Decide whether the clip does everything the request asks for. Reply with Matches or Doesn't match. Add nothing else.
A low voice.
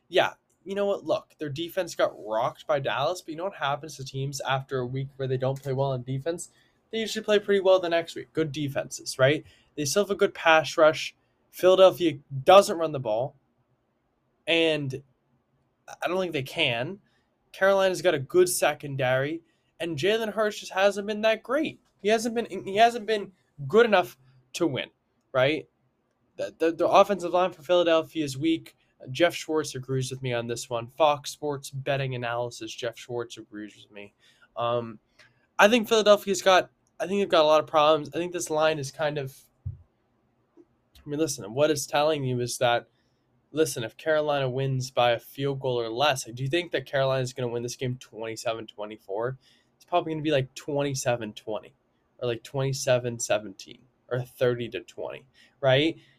Doesn't match